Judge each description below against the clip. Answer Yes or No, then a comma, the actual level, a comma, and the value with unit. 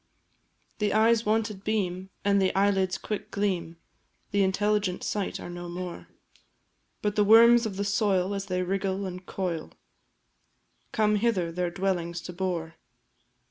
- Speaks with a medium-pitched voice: No, high, 195 Hz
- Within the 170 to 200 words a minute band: No, average, 140 wpm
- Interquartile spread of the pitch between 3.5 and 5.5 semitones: No, narrow, 2.4 semitones